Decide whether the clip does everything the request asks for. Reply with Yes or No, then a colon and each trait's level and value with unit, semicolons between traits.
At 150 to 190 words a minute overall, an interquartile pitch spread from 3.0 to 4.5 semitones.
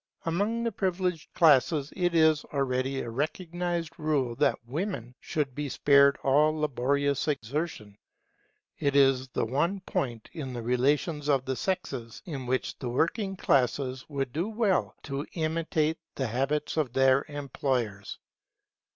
No: average, 140 wpm; average, 3.8 semitones